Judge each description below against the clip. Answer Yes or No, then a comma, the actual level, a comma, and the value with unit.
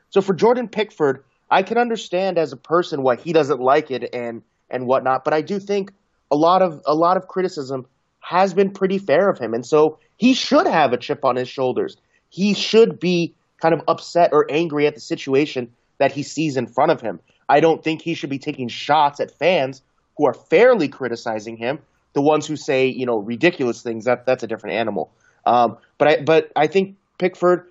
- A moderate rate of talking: No, fast, 210 wpm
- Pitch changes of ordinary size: No, wide, 6.0 semitones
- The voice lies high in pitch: No, medium, 155 Hz